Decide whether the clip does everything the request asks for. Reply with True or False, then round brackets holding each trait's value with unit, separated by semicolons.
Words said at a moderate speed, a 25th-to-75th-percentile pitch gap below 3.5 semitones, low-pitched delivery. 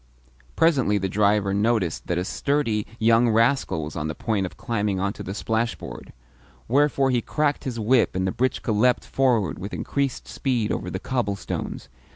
False (170 wpm; 4.3 semitones; 110 Hz)